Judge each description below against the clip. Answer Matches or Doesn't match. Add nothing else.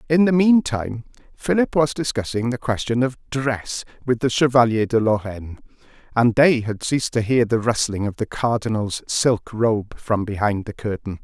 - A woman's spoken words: Doesn't match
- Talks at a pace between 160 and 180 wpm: Matches